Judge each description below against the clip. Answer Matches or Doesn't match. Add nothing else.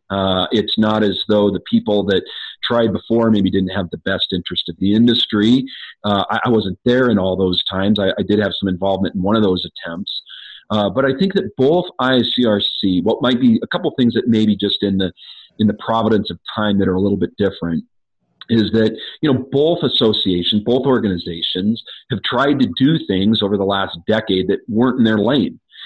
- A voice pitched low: Matches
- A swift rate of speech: Matches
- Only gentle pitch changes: Doesn't match